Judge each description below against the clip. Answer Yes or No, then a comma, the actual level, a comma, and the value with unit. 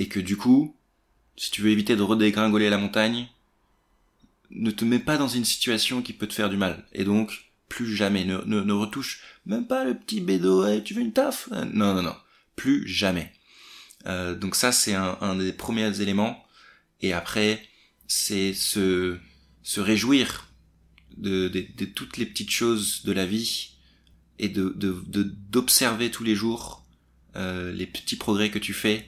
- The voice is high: No, low, 105 Hz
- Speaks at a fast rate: No, average, 180 wpm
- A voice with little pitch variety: No, average, 3.4 semitones